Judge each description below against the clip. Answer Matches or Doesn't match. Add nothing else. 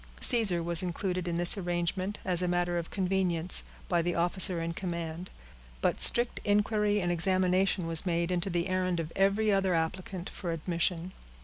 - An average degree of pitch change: Doesn't match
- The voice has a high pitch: Doesn't match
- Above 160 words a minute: Matches